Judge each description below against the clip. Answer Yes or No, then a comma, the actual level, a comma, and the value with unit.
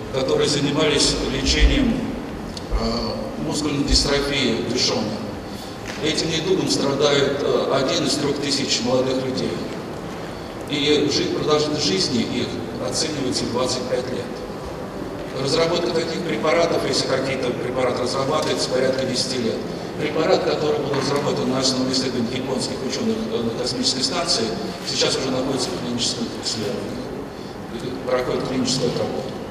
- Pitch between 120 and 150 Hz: Yes, medium, 140 Hz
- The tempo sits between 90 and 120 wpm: Yes, average, 115 wpm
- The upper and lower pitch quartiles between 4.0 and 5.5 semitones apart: No, narrow, 2.5 semitones